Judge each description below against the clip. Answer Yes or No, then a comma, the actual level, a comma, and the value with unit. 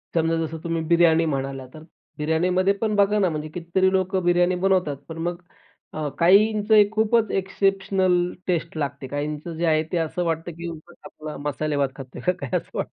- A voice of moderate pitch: Yes, medium, 170 Hz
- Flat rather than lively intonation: No, average, 3.3 semitones